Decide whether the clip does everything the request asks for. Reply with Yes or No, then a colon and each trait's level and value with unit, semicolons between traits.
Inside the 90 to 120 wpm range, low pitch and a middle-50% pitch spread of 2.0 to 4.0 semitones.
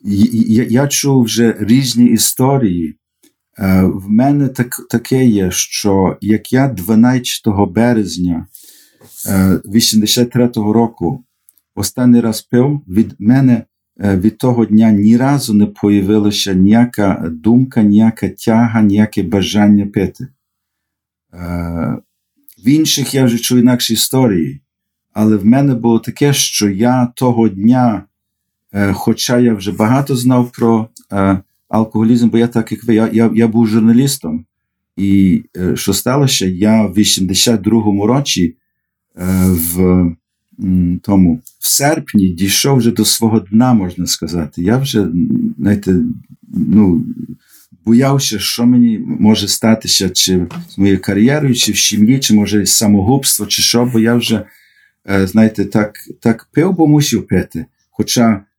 No: average, 130 wpm; low, 110 Hz; average, 3.5 semitones